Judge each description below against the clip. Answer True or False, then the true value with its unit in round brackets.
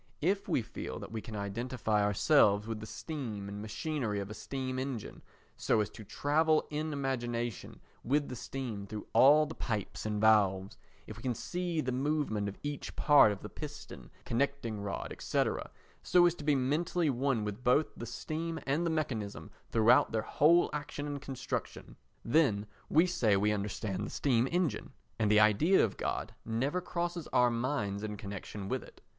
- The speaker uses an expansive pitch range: True (5.7 semitones)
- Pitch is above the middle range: False (125 Hz)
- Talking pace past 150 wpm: True (180 wpm)